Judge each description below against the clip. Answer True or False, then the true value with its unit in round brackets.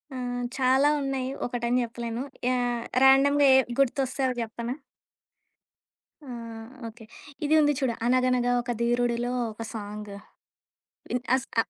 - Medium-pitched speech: False (245 Hz)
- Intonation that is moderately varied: False (1.8 semitones)